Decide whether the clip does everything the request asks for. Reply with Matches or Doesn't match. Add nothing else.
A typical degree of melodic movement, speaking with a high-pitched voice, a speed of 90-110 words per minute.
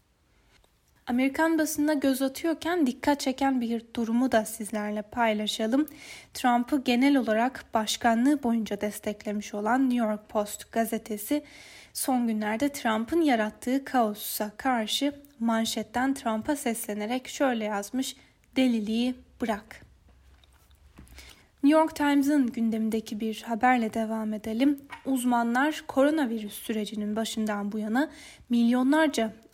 Matches